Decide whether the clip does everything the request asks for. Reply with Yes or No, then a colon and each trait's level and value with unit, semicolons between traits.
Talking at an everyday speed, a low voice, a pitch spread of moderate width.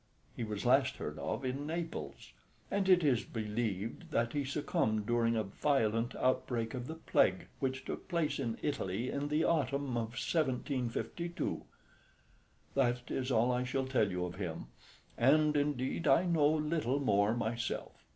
Yes: average, 155 wpm; low, 130 Hz; average, 4.2 semitones